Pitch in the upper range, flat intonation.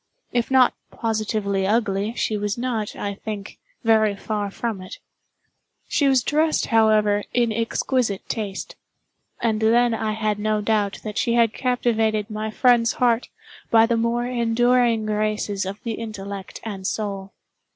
Yes: high, 220 Hz; narrow, 2.1 semitones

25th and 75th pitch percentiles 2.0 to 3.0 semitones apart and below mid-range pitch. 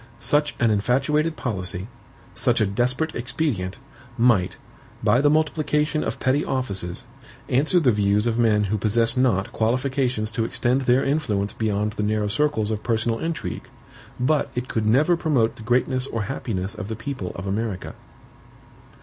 No: average, 4.4 semitones; low, 120 Hz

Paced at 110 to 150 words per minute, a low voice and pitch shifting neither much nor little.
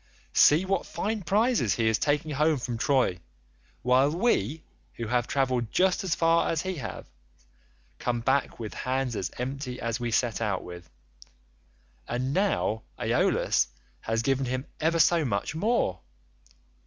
No: average, 145 wpm; low, 130 Hz; wide, 6.1 semitones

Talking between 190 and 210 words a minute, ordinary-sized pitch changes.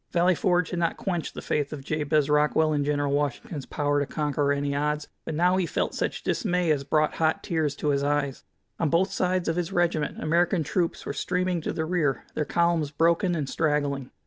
Yes: fast, 205 wpm; average, 3.0 semitones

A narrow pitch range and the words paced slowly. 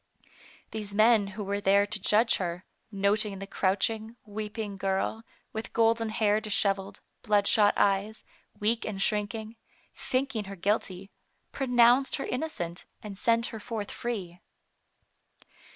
Yes: narrow, 2.3 semitones; slow, 125 wpm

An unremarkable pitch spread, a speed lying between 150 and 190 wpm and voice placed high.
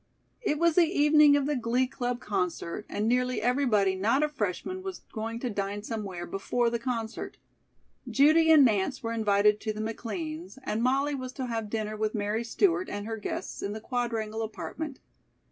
Yes: average, 4.8 semitones; average, 180 wpm; high, 235 Hz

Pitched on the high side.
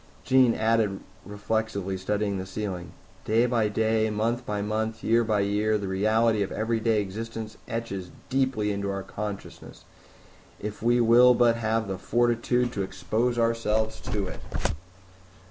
No: low, 110 Hz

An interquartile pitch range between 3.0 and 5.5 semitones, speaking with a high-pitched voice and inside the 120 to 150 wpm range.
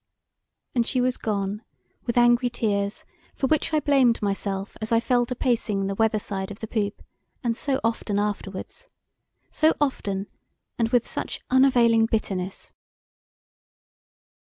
Yes: average, 3.5 semitones; high, 225 Hz; average, 140 wpm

